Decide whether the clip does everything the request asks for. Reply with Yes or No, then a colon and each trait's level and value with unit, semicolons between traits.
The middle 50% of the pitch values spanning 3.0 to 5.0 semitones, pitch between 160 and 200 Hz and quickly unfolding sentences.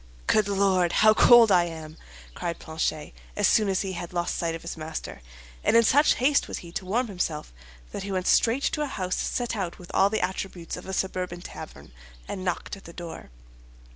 Yes: average, 3.6 semitones; medium, 185 Hz; fast, 210 wpm